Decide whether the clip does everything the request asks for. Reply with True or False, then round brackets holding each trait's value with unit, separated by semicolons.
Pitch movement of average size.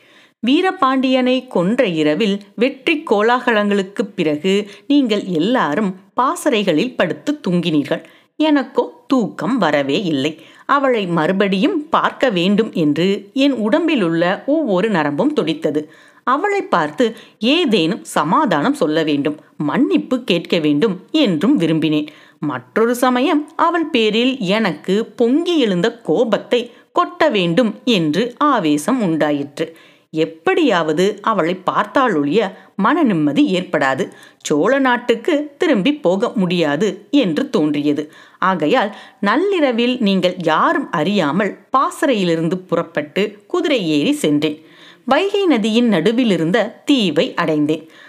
False (8.1 semitones)